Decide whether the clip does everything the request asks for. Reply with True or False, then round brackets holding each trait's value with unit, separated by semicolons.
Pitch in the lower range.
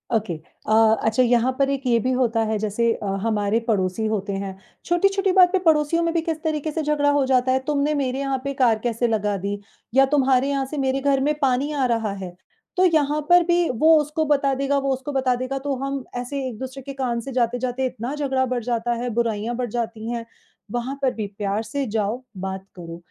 False (255 Hz)